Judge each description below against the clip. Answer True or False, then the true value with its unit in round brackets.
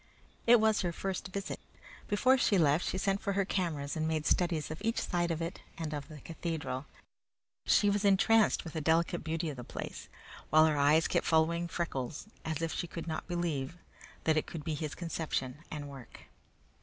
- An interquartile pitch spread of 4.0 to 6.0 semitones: False (3.1 semitones)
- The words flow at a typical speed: True (195 wpm)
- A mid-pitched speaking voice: True (165 Hz)